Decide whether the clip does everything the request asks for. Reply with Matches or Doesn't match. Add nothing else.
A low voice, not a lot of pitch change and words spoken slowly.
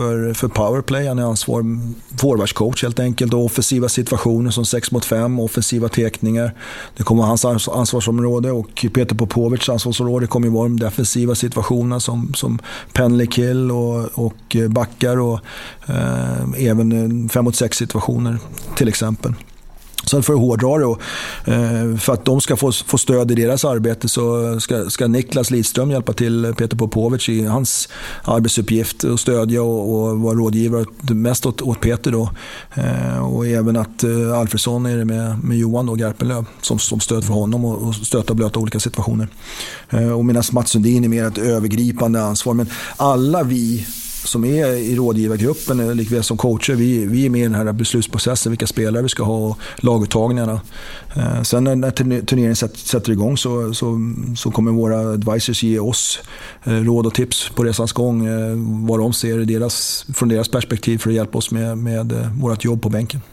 Doesn't match